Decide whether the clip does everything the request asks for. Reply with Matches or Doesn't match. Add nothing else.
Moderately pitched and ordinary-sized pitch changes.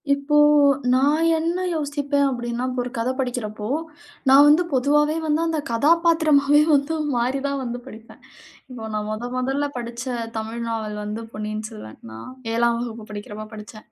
Doesn't match